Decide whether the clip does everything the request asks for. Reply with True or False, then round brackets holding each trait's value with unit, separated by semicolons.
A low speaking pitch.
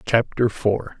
True (115 Hz)